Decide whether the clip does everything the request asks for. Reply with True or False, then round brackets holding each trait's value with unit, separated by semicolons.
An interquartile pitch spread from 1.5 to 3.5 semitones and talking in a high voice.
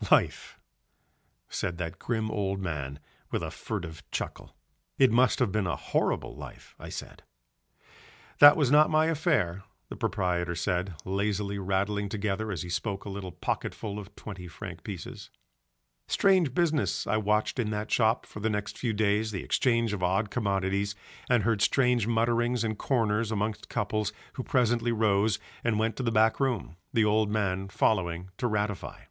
False (3.1 semitones; 105 Hz)